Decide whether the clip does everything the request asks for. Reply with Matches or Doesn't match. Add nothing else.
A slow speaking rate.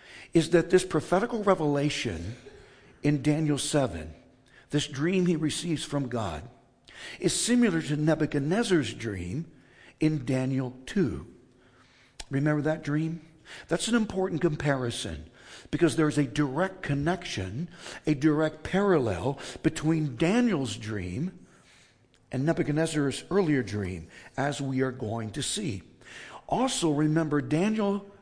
Matches